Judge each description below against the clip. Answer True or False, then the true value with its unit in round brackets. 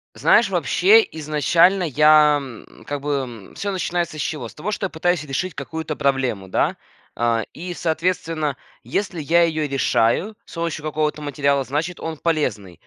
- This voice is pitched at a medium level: True (155 Hz)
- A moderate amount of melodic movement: True (3.3 semitones)